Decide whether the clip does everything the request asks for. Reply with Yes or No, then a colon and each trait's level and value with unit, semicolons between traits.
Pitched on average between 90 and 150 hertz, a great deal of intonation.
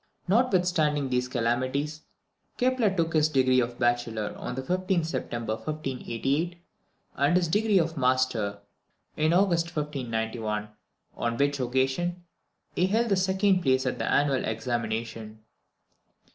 Yes: medium, 140 Hz; wide, 6.4 semitones